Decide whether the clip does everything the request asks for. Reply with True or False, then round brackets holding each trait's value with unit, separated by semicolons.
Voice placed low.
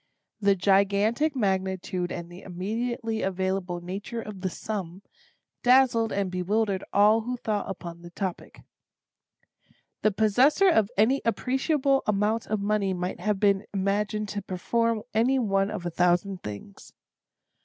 False (200 Hz)